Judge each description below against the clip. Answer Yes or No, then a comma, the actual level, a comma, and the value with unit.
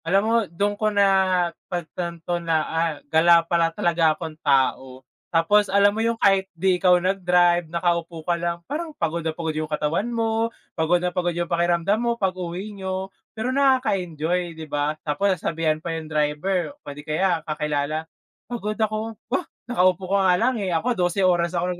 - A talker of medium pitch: Yes, medium, 175 Hz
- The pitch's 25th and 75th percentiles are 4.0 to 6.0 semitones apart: No, average, 3.3 semitones